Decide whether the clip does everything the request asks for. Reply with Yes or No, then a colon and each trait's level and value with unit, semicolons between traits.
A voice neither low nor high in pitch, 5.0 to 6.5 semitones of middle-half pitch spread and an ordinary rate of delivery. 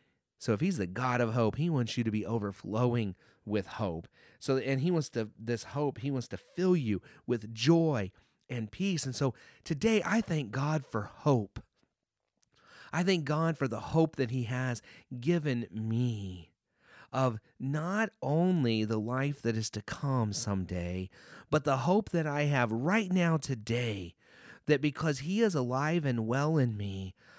No: low, 130 Hz; wide, 5.6 semitones; average, 170 wpm